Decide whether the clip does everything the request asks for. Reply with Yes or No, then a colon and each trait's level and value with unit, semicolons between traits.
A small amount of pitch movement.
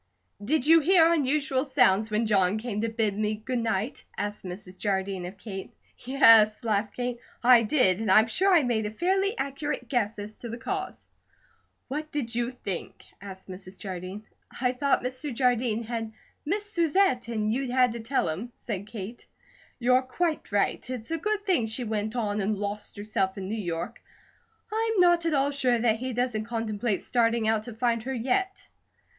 No: average, 4.2 semitones